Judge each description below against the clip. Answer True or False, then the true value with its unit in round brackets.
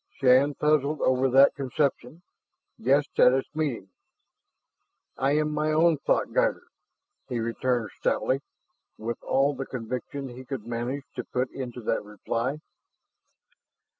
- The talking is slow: True (125 wpm)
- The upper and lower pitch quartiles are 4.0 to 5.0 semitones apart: False (2.9 semitones)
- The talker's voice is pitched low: True (130 Hz)